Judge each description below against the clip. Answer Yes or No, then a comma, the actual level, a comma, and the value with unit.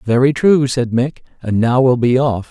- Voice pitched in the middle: No, low, 125 Hz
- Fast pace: Yes, fast, 215 wpm